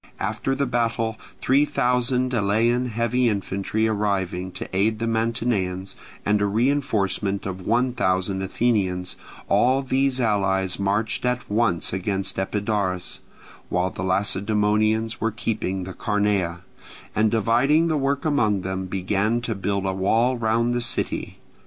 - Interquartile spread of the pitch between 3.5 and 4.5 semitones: Yes, average, 3.8 semitones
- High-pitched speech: No, low, 110 Hz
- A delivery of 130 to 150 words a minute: Yes, slow, 135 wpm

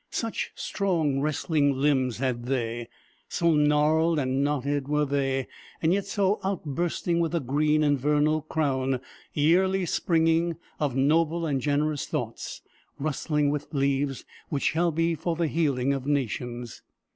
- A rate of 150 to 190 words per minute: No, slow, 135 wpm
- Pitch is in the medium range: Yes, medium, 150 Hz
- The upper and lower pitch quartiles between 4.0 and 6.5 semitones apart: No, average, 3.2 semitones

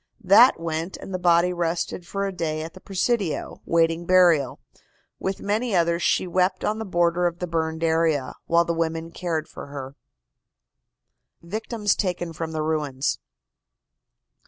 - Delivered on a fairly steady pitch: Yes, narrow, 2.2 semitones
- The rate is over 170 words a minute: No, average, 155 wpm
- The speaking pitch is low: No, medium, 170 Hz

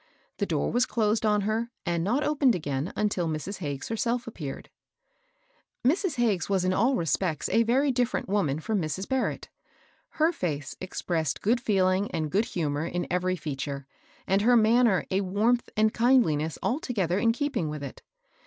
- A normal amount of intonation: No, wide, 6.2 semitones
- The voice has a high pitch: Yes, high, 200 Hz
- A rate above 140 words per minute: Yes, average, 170 wpm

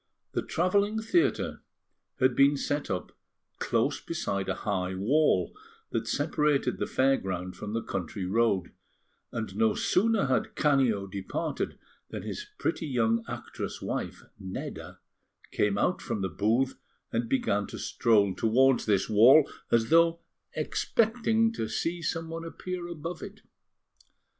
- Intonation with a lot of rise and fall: Yes, wide, 8.3 semitones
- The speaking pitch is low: Yes, low, 130 Hz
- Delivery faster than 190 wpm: No, slow, 135 wpm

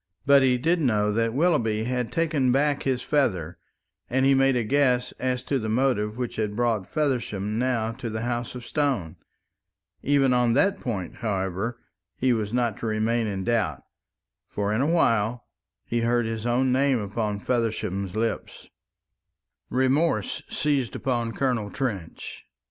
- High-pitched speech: No, low, 120 Hz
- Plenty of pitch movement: No, average, 3.5 semitones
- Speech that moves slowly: No, average, 155 wpm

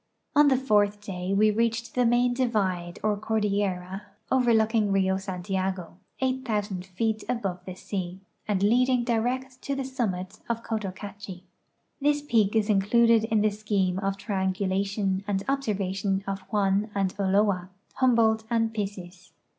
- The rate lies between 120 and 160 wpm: Yes, average, 140 wpm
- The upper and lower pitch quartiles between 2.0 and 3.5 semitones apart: Yes, average, 3.2 semitones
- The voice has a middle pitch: No, high, 205 Hz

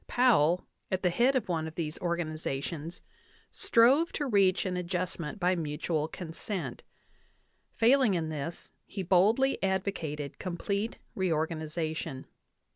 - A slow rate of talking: Yes, slow, 120 wpm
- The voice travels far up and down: No, average, 4.0 semitones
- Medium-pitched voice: Yes, medium, 175 Hz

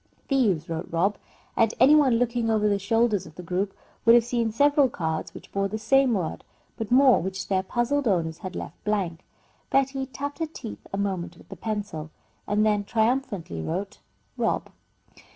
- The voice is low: No, high, 210 Hz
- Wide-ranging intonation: No, average, 4.7 semitones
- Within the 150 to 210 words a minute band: Yes, average, 180 wpm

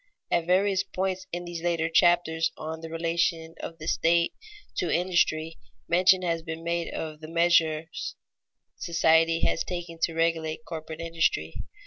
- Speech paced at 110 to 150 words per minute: Yes, average, 145 wpm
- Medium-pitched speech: Yes, medium, 165 Hz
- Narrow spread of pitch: Yes, narrow, 1.1 semitones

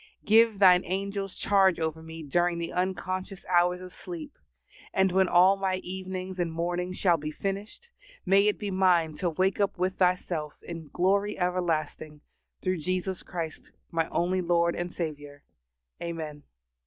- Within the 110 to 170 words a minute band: Yes, average, 155 wpm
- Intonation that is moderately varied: No, narrow, 2.2 semitones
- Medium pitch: Yes, medium, 180 Hz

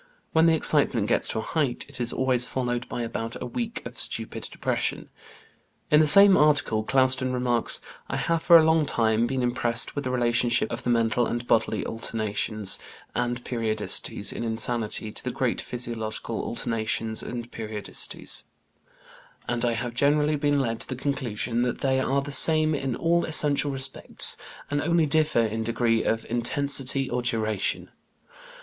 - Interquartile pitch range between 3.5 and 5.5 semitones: Yes, average, 3.8 semitones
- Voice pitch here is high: No, low, 125 Hz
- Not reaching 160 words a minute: No, average, 165 wpm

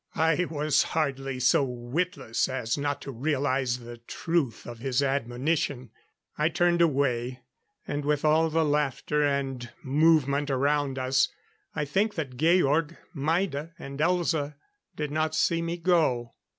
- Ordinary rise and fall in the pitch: Yes, average, 3.5 semitones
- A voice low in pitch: No, medium, 145 Hz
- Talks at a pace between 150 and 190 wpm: No, slow, 135 wpm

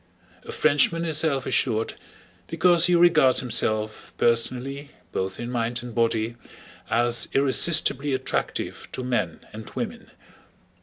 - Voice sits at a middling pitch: No, low, 125 Hz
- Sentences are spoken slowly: Yes, slow, 120 wpm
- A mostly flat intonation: No, average, 4.3 semitones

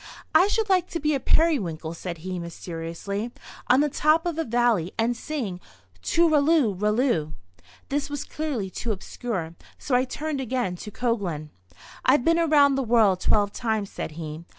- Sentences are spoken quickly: No, average, 165 wpm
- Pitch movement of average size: No, wide, 8.0 semitones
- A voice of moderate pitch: No, high, 240 Hz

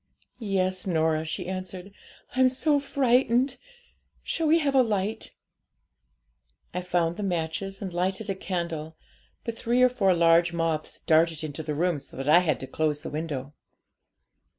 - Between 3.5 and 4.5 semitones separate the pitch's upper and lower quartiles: No, wide, 5.4 semitones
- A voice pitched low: No, medium, 180 Hz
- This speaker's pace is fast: No, average, 155 wpm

